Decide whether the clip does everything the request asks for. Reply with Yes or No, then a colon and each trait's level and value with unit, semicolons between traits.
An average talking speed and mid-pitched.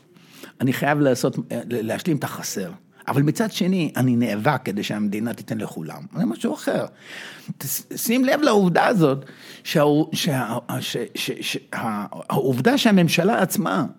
Yes: average, 110 wpm; medium, 155 Hz